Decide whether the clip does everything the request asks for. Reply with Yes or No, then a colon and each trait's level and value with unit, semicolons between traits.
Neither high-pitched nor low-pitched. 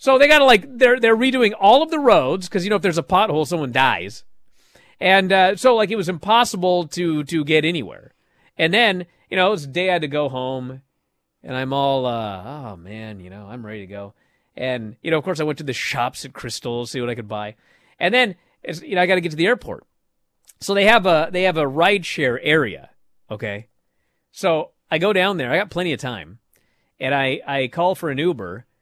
Yes: medium, 160 Hz